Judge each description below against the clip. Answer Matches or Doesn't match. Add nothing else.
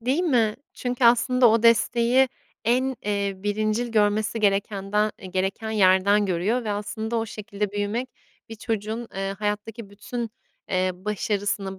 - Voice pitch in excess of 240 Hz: Doesn't match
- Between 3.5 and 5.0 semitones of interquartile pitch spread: Doesn't match